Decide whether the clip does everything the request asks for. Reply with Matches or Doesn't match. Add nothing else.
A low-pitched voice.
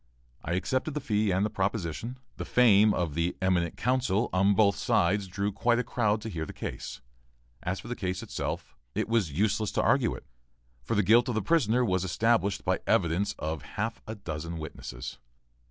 Matches